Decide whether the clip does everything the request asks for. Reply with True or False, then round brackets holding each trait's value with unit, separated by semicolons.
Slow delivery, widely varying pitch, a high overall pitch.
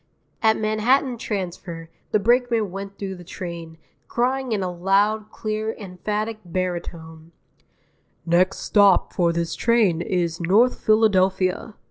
False (120 wpm; 3.7 semitones; 195 Hz)